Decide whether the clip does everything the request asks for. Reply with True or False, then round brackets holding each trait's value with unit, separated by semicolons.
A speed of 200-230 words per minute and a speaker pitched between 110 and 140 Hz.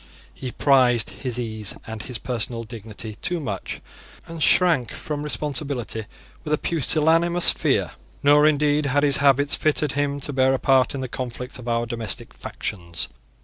False (160 wpm; 135 Hz)